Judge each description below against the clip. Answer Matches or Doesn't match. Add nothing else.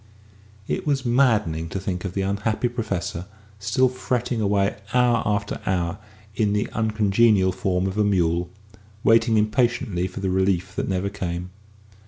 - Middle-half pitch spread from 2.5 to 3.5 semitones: Matches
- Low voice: Matches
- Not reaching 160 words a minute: Matches